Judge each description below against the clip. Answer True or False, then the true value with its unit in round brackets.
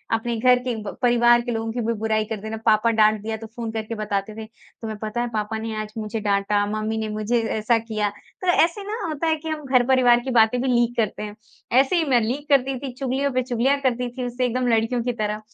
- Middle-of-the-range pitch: False (230 Hz)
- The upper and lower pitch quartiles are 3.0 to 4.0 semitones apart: False (2.6 semitones)